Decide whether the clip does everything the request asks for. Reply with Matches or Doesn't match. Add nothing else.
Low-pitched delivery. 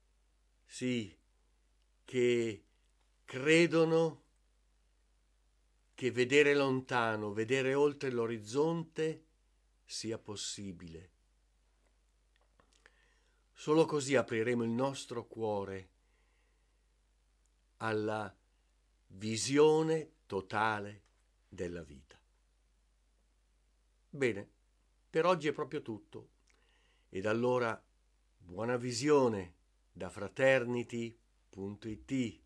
Matches